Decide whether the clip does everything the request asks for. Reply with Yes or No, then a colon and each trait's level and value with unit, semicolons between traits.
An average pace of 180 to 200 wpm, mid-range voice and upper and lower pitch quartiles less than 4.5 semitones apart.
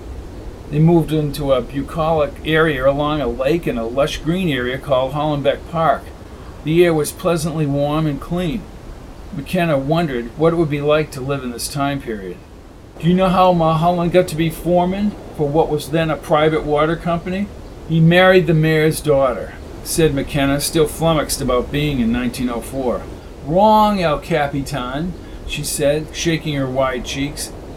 No: average, 165 wpm; medium, 150 Hz; average, 3.5 semitones